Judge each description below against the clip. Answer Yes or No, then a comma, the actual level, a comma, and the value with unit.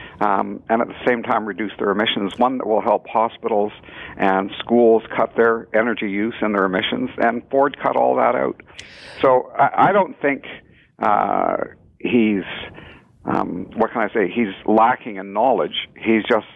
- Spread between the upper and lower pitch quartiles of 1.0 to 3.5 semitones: Yes, narrow, 2.5 semitones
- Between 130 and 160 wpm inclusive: No, average, 170 wpm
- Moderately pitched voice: No, low, 110 Hz